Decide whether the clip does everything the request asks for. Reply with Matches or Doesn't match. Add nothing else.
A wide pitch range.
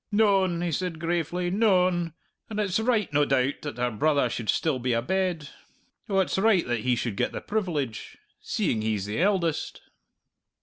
Matches